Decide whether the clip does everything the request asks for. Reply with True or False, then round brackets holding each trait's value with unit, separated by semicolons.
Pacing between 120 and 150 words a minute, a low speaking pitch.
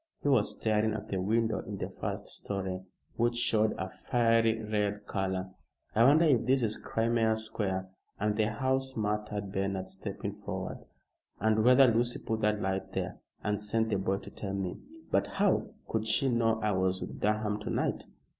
False (180 wpm; 105 Hz)